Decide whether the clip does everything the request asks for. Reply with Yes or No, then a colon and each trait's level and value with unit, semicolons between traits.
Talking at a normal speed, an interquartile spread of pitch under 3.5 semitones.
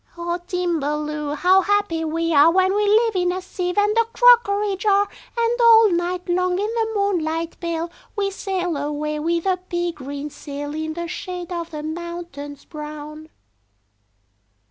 No: average, 160 wpm; average, 4.1 semitones